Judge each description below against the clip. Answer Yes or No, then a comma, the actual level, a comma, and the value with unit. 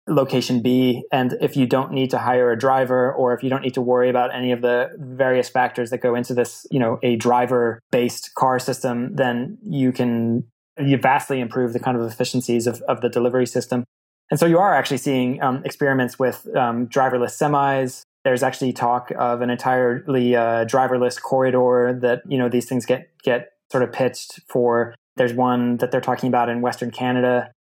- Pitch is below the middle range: Yes, low, 125 Hz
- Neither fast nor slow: Yes, average, 195 wpm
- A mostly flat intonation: Yes, narrow, 1.2 semitones